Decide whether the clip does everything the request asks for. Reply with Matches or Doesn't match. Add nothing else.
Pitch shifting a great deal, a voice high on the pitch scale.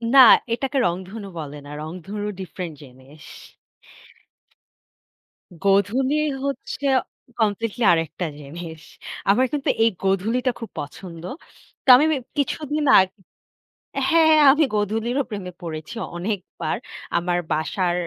Matches